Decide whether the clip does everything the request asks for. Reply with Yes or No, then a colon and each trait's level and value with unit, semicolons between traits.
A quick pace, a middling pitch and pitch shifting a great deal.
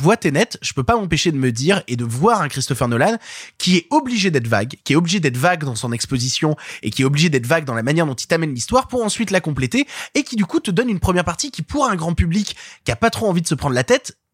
Yes: fast, 290 wpm; medium, 165 Hz; wide, 7.4 semitones